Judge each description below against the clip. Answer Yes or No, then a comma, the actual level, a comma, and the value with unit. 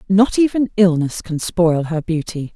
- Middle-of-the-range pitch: Yes, medium, 180 Hz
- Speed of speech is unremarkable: Yes, average, 165 wpm